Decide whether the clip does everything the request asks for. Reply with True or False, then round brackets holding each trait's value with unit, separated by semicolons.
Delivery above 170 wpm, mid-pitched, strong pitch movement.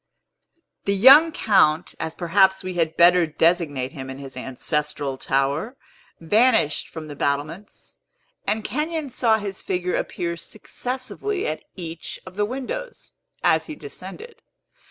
False (135 wpm; 180 Hz; 6.8 semitones)